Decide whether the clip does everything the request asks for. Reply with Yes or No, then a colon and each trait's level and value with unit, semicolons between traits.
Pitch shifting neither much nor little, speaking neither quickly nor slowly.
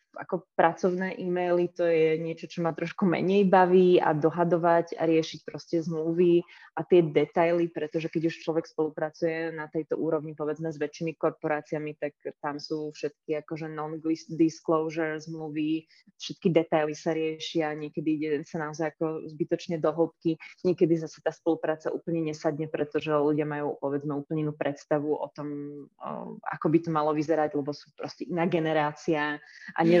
No: narrow, 1.7 semitones; average, 155 wpm